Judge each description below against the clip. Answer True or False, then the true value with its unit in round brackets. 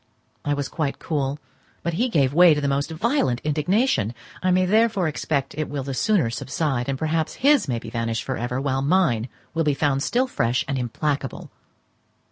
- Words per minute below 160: False (190 wpm)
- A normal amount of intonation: True (4.5 semitones)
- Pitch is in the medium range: True (145 Hz)